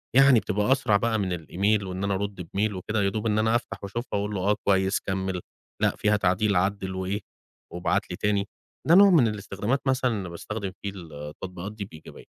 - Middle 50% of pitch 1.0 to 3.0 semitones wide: Yes, narrow, 2.4 semitones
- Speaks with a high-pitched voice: No, low, 100 Hz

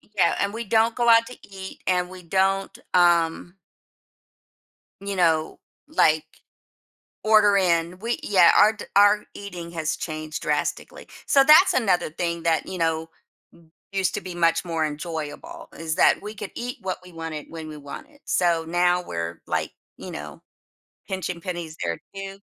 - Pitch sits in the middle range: Yes, medium, 180 Hz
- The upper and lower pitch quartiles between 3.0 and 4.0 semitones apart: Yes, average, 3.6 semitones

